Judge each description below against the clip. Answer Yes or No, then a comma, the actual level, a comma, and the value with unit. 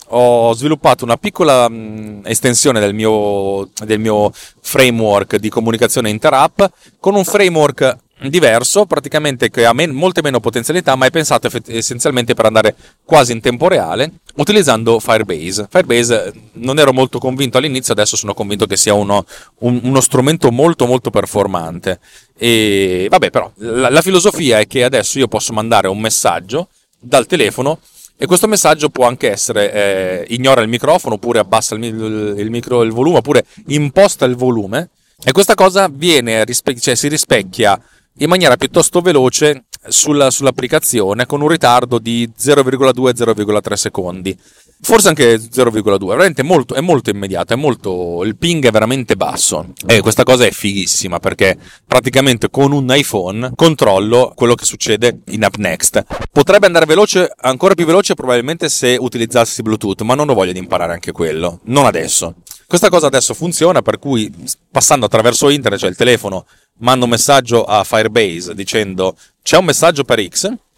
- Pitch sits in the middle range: No, low, 125 Hz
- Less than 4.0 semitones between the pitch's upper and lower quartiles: No, average, 5.3 semitones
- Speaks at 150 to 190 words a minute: Yes, average, 160 wpm